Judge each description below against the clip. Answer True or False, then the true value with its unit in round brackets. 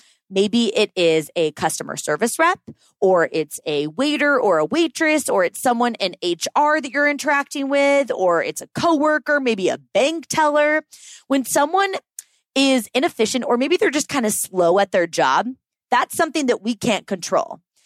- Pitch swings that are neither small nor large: False (7.2 semitones)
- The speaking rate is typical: True (170 wpm)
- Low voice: False (270 Hz)